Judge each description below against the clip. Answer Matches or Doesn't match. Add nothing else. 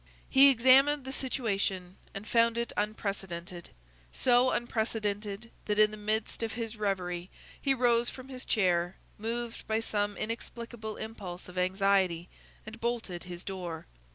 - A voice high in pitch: Matches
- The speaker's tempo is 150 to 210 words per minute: Doesn't match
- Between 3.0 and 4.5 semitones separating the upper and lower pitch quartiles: Matches